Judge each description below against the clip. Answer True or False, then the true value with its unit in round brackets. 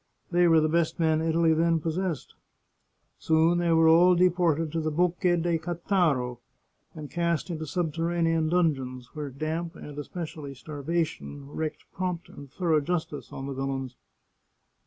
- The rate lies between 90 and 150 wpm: True (145 wpm)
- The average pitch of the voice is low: False (160 Hz)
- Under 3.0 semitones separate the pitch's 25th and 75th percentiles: True (2.5 semitones)